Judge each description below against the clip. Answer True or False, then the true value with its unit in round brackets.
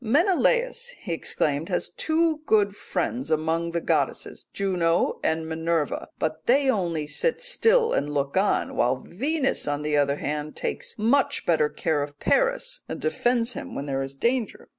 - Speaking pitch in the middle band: True (175 Hz)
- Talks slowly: False (165 wpm)